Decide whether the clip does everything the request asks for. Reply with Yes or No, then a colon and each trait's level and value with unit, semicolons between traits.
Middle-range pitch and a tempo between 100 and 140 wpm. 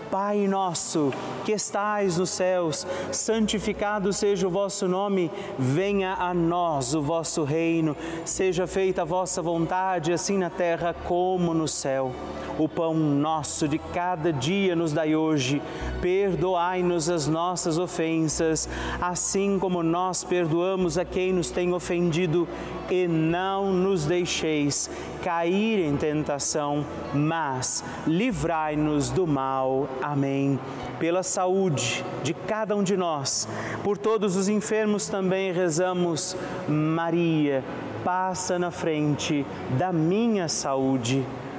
Yes: medium, 175 Hz; slow, 120 wpm